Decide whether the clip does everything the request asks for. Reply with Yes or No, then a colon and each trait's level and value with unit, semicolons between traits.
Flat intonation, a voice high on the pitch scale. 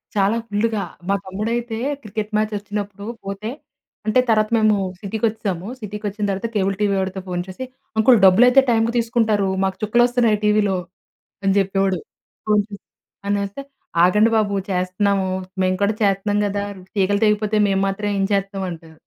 Yes: narrow, 1.8 semitones; high, 205 Hz